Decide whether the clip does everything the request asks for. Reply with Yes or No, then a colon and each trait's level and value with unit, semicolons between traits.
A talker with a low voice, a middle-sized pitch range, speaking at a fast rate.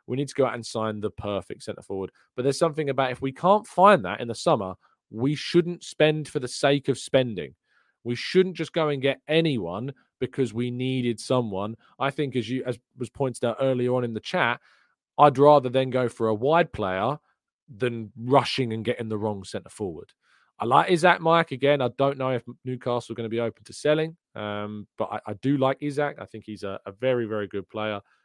Yes: low, 125 Hz; average, 4.1 semitones; fast, 220 wpm